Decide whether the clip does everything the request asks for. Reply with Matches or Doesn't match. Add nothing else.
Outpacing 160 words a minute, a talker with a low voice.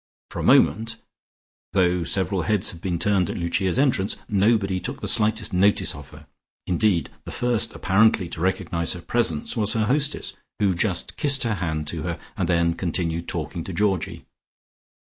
Matches